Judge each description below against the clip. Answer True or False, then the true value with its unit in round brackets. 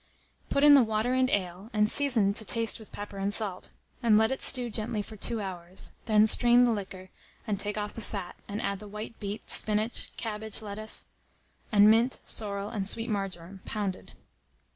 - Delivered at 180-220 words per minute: True (185 wpm)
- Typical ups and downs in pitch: False (2.2 semitones)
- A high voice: True (210 Hz)